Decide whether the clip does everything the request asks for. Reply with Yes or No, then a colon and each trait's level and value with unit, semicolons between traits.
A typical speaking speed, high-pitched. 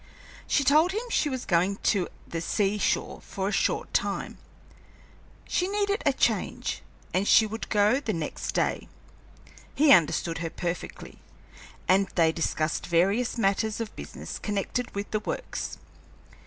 Yes: average, 145 wpm; high, 205 Hz